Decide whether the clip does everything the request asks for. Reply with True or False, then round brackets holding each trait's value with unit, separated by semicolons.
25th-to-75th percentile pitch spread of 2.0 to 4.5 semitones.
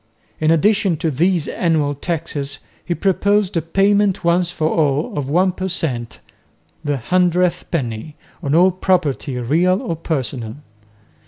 True (4.2 semitones)